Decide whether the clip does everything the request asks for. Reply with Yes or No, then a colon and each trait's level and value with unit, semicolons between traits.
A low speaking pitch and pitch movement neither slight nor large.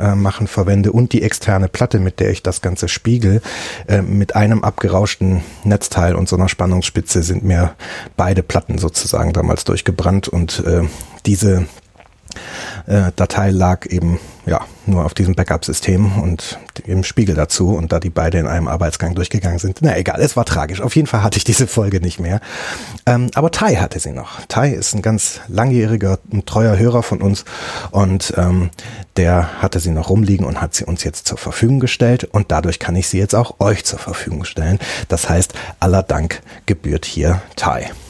Yes: very low, 95 Hz; average, 3.2 semitones